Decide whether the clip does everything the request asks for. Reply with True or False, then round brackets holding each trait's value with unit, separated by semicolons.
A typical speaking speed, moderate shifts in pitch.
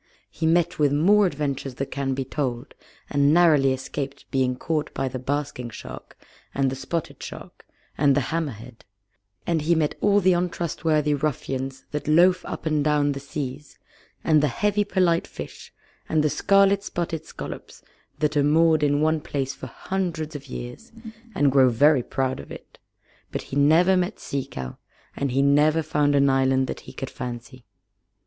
True (170 wpm; 3.3 semitones)